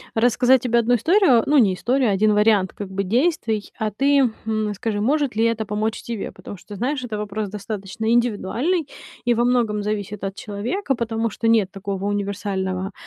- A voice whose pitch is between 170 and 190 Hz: No, high, 220 Hz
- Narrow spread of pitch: No, average, 3.0 semitones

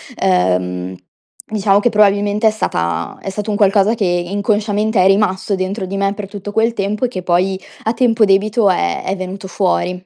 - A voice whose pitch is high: Yes, high, 195 Hz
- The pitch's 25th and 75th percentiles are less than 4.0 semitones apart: Yes, narrow, 2.4 semitones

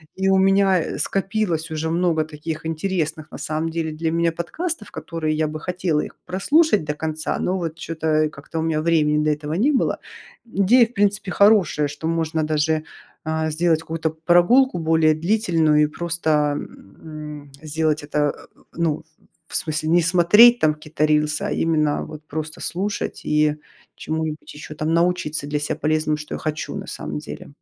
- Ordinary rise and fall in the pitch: No, narrow, 2.3 semitones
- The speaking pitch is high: No, medium, 160 Hz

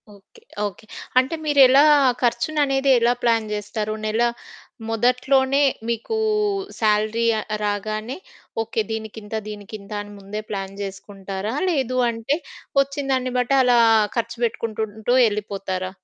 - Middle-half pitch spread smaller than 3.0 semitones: No, average, 3.4 semitones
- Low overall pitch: No, high, 225 Hz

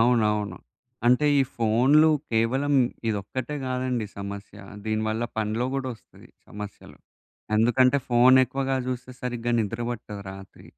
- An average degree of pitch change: Yes, average, 3.1 semitones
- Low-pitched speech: Yes, low, 120 Hz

